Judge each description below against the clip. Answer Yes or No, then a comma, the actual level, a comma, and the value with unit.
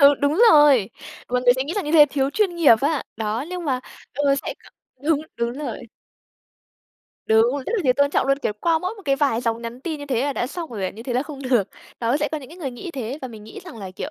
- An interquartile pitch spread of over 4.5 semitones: No, average, 3.9 semitones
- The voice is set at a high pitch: Yes, very high, 275 Hz